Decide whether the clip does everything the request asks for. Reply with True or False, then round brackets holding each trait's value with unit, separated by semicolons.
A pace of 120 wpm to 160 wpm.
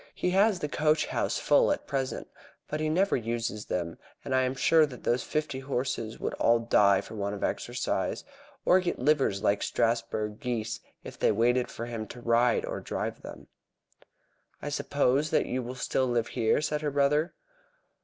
False (185 wpm)